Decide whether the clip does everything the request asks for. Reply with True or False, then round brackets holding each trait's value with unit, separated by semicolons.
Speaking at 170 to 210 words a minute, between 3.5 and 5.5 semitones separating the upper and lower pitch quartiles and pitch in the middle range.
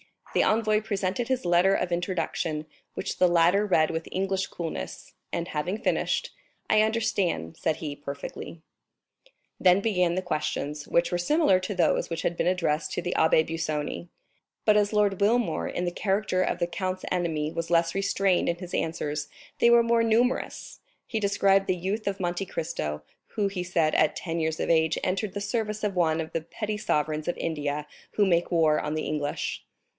True (185 wpm; 3.8 semitones; 180 Hz)